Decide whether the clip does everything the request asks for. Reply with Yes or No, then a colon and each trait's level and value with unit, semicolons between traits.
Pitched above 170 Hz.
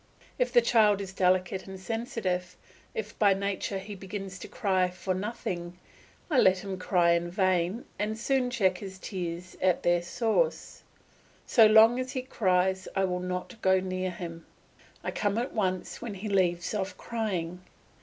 Yes: high, 190 Hz